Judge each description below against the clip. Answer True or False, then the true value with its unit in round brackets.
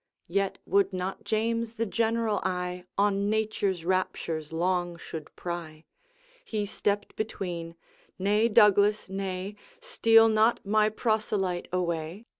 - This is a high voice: True (200 Hz)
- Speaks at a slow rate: True (120 wpm)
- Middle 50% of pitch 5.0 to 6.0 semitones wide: False (3.2 semitones)